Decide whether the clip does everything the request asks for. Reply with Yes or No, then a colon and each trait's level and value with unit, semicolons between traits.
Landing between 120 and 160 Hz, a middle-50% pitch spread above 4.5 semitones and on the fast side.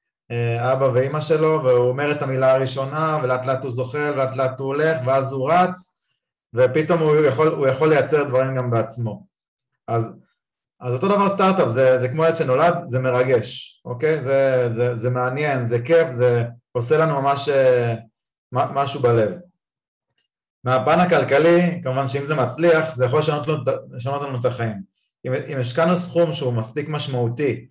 No: low, 135 Hz; average, 3.7 semitones; fast, 160 wpm